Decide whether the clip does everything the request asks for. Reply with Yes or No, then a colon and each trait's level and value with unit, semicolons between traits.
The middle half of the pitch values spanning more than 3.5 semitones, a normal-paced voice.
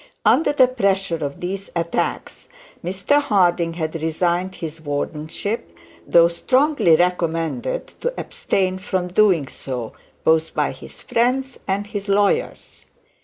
No: average, 4.1 semitones; slow, 120 wpm